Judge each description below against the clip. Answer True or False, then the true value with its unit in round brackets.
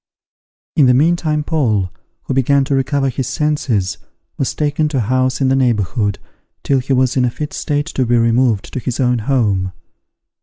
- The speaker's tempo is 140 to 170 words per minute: False (185 wpm)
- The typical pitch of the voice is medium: False (130 Hz)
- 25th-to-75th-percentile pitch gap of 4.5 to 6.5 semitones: False (3.3 semitones)